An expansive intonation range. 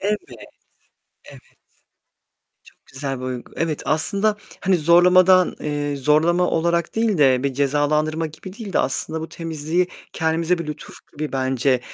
No: average, 3.5 semitones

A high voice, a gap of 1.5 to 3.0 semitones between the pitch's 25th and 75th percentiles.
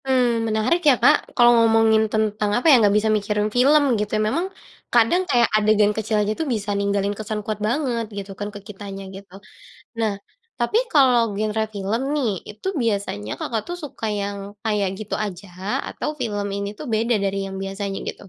Yes: high, 215 Hz; average, 2.7 semitones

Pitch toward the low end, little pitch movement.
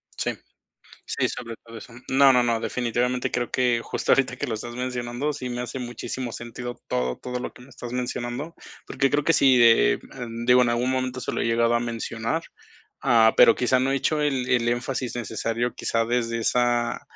Yes: low, 120 Hz; narrow, 1.5 semitones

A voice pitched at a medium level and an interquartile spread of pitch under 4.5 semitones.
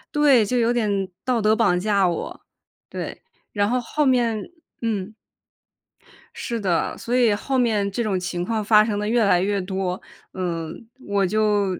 No: high, 210 Hz; average, 3.2 semitones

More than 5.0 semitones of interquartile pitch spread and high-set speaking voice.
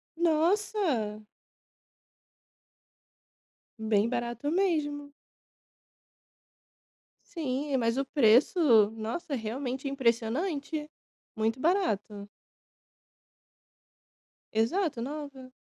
Yes: wide, 5.4 semitones; very high, 270 Hz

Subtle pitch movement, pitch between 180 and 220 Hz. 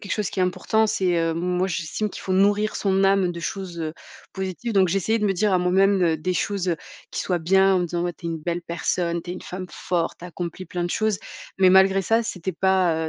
Yes: narrow, 2.1 semitones; medium, 185 Hz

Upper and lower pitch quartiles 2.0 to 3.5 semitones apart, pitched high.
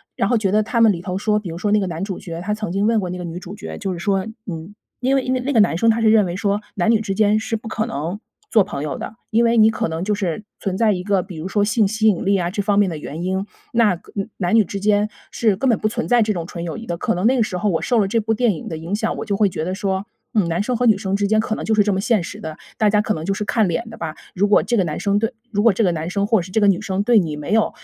Yes: average, 3.2 semitones; high, 205 Hz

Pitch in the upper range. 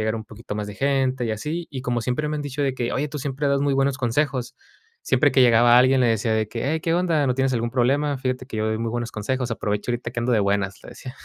No: low, 125 Hz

